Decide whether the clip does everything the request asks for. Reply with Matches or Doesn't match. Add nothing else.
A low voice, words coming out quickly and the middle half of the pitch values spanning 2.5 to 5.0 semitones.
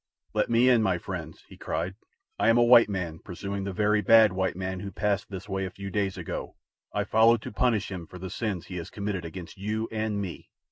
Matches